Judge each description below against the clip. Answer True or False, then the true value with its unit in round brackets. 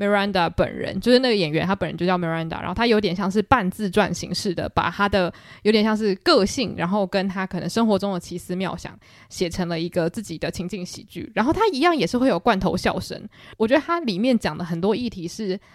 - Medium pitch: False (195 Hz)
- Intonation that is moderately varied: True (3.5 semitones)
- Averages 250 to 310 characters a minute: False (385 characters per minute)